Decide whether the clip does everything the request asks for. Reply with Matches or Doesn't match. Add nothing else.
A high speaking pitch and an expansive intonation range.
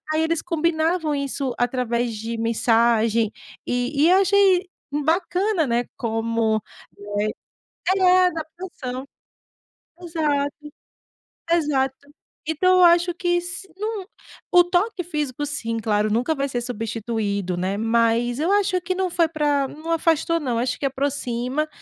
Matches